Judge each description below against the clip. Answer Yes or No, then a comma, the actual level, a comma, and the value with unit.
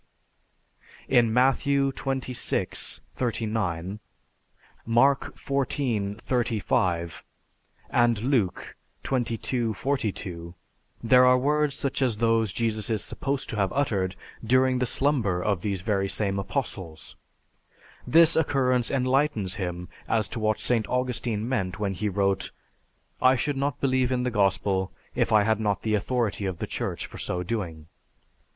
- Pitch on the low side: Yes, low, 115 Hz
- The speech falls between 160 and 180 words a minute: No, slow, 135 wpm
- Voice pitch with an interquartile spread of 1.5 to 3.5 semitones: No, average, 4.6 semitones